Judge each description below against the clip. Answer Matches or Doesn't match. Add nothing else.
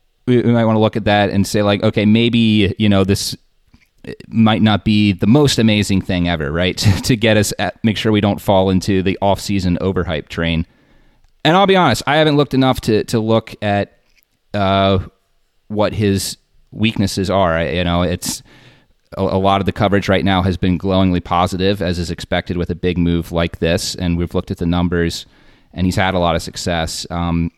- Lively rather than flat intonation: Doesn't match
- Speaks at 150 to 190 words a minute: Doesn't match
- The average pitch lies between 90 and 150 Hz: Matches